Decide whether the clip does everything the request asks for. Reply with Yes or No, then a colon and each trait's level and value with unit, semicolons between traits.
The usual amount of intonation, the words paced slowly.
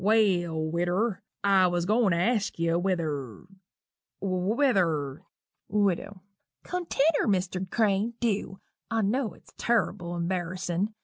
Yes: average, 3.9 semitones; slow, 120 wpm